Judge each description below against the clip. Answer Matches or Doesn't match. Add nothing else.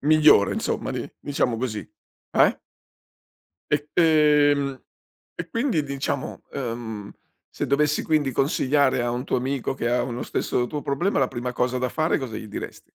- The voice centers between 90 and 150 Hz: Matches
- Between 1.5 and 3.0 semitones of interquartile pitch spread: Doesn't match